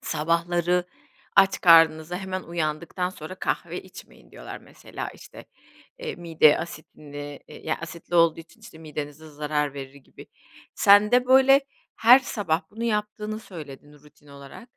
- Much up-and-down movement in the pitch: No, average, 4.8 semitones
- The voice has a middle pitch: Yes, medium, 165 Hz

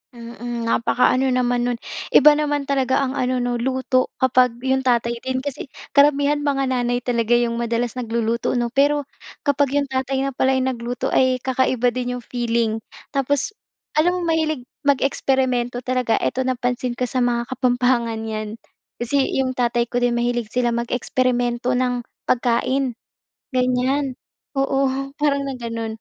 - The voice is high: Yes, very high, 250 Hz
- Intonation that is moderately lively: No, narrow, 1.9 semitones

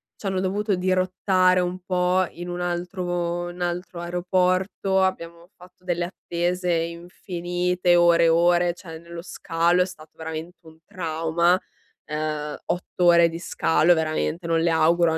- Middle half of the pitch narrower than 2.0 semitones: Yes, narrow, 1.4 semitones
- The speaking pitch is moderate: Yes, medium, 175 Hz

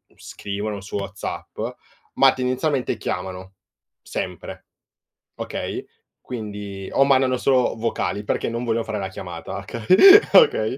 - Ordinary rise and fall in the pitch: Yes, average, 4.2 semitones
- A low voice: Yes, low, 110 Hz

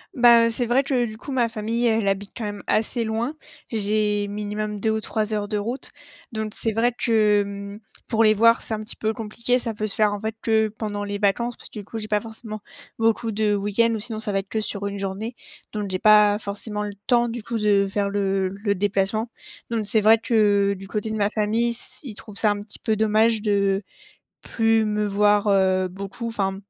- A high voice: Yes, high, 215 Hz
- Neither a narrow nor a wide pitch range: No, narrow, 1.8 semitones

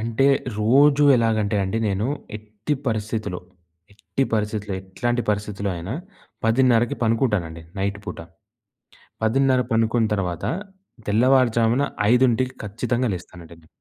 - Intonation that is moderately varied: Yes, average, 3.1 semitones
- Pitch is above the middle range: No, low, 110 Hz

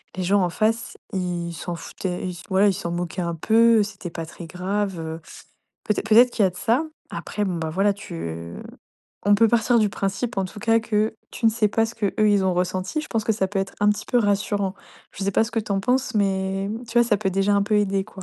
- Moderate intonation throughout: Yes, average, 3.0 semitones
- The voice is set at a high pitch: Yes, high, 200 Hz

